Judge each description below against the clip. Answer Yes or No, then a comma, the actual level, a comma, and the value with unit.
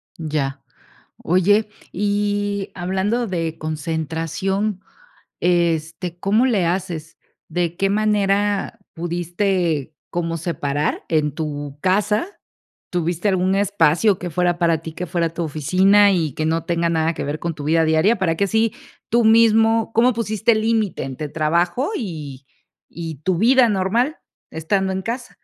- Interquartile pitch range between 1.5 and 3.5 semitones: No, average, 4.1 semitones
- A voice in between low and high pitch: Yes, medium, 180 Hz